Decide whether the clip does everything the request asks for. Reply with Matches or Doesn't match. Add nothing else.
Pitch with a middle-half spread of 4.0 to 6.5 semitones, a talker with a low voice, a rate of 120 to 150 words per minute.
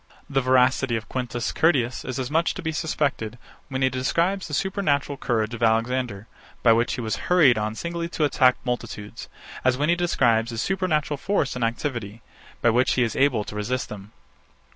Doesn't match